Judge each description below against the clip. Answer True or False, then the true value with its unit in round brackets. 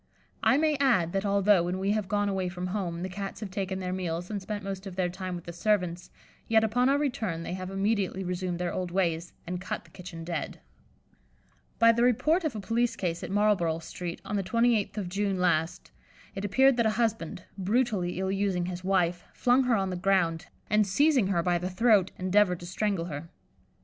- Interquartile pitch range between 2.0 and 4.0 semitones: True (3.1 semitones)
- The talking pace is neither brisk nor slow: False (210 wpm)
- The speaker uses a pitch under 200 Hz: True (190 Hz)